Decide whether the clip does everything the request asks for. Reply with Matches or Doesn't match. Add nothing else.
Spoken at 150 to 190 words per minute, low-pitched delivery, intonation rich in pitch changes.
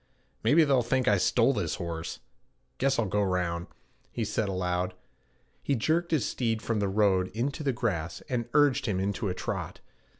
Matches